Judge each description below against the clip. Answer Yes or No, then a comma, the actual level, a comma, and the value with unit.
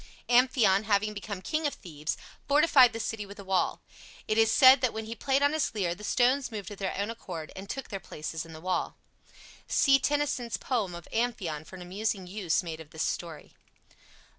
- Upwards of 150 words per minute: Yes, fast, 205 wpm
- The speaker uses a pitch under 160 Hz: No, high, 210 Hz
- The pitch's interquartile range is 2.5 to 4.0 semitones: No, wide, 5.4 semitones